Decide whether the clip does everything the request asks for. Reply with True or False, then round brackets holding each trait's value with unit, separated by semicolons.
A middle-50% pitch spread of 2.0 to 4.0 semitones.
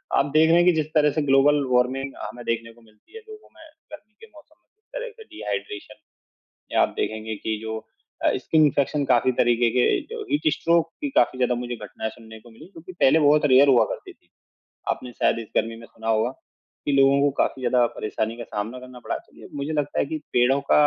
False (5.2 semitones)